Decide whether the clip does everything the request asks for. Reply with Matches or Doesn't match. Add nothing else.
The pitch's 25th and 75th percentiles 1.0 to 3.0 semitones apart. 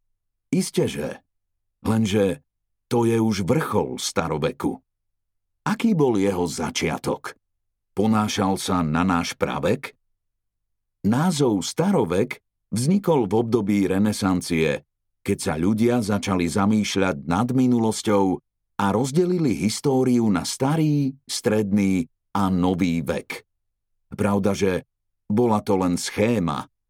Matches